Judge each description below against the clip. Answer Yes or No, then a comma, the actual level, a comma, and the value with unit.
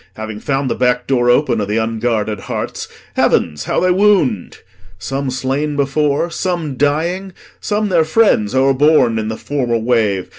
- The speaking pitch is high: No, low, 130 Hz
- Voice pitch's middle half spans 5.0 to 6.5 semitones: Yes, wide, 5.4 semitones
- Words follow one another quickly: No, average, 155 wpm